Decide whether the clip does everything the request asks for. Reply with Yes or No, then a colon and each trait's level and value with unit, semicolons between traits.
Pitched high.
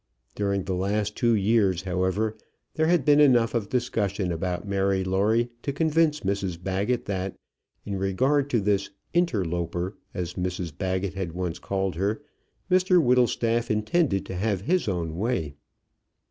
No: low, 100 Hz